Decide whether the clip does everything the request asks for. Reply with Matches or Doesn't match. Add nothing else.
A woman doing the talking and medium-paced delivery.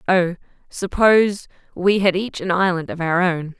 Matches